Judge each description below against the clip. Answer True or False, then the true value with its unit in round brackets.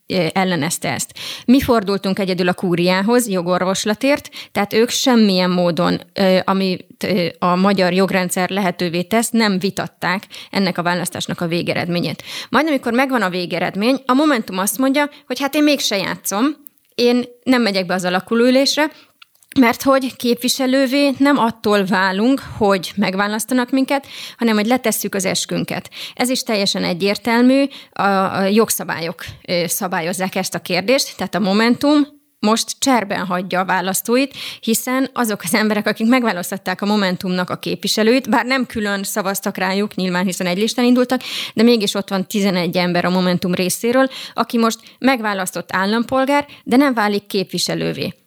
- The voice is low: False (205 Hz)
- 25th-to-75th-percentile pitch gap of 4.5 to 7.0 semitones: True (5.2 semitones)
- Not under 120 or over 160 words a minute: True (145 wpm)